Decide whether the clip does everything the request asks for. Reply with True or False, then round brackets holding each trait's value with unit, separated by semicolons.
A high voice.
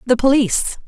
True (250 Hz)